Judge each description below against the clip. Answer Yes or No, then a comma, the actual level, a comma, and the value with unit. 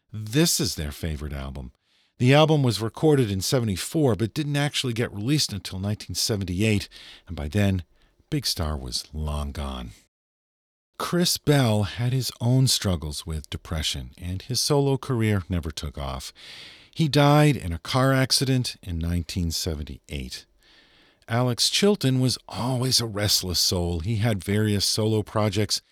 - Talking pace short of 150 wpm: Yes, average, 140 wpm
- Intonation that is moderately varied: No, wide, 7.1 semitones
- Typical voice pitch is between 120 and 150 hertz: No, low, 105 Hz